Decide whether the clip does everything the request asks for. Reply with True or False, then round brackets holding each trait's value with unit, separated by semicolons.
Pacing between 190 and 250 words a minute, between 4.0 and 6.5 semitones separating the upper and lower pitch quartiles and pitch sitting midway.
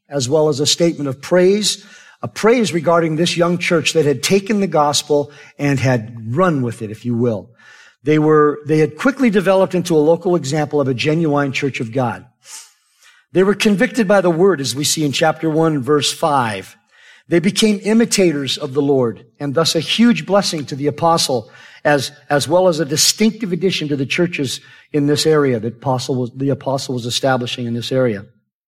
True (195 wpm; 4.5 semitones; 150 Hz)